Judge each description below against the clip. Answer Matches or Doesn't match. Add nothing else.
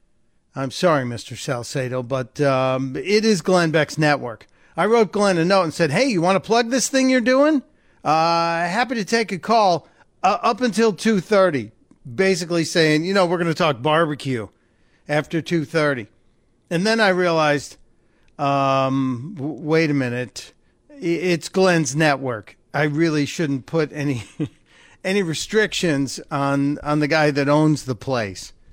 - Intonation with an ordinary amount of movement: Doesn't match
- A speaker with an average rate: Matches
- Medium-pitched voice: Matches